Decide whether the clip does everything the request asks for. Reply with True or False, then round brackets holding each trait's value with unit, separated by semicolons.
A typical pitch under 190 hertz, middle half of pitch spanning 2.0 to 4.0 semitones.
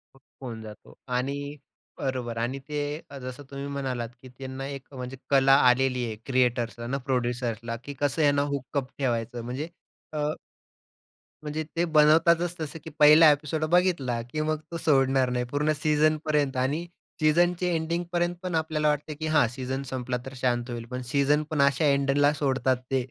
True (140 Hz; 3.2 semitones)